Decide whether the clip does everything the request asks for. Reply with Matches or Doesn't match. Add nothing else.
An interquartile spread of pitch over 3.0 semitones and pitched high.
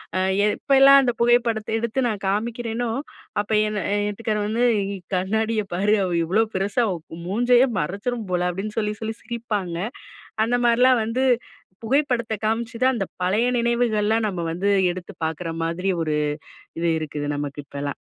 Matches